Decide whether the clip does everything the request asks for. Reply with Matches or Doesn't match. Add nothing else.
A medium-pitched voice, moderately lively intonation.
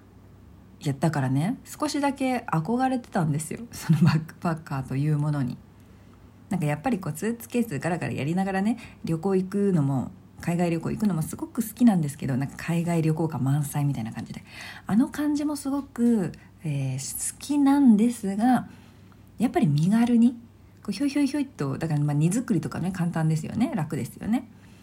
Doesn't match